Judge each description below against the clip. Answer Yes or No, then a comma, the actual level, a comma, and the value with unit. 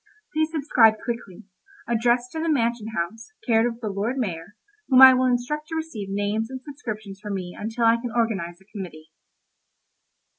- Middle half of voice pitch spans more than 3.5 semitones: Yes, average, 3.9 semitones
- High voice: Yes, high, 230 Hz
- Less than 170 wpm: No, average, 175 wpm